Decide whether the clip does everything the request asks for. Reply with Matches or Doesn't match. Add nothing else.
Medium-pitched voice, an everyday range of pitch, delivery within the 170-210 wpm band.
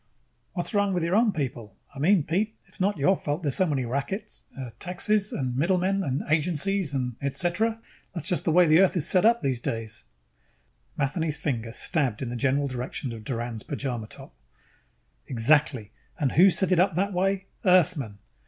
Doesn't match